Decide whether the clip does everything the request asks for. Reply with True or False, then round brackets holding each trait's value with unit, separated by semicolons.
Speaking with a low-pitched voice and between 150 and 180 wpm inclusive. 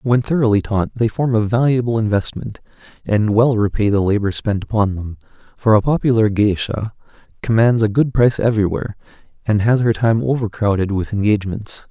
True (110 Hz; 160 wpm)